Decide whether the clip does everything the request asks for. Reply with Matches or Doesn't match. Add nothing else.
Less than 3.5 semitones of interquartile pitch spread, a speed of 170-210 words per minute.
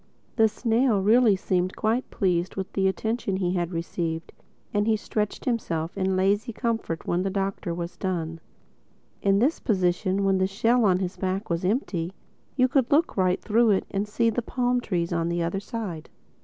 Doesn't match